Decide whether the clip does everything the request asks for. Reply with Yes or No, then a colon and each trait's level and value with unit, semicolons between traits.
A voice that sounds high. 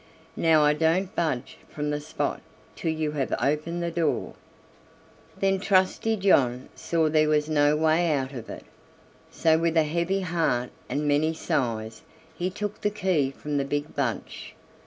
No: medium, 155 Hz